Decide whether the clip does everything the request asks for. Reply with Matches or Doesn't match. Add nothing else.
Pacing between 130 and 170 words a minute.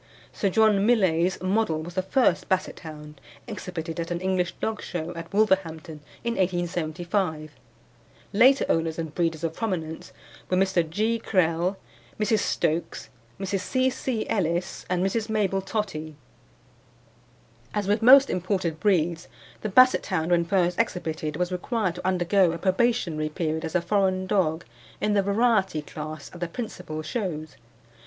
Matches